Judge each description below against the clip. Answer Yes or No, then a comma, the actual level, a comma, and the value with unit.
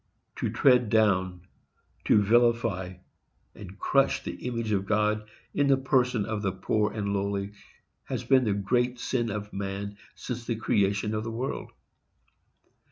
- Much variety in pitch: No, average, 3.2 semitones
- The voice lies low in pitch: Yes, low, 105 Hz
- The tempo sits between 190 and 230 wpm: No, average, 150 wpm